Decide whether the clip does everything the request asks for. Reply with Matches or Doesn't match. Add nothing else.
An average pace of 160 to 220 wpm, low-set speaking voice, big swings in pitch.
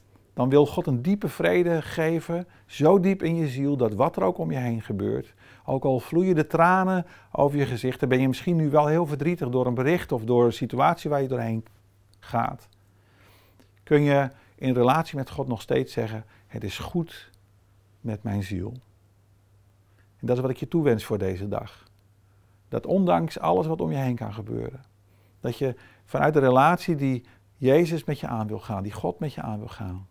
Matches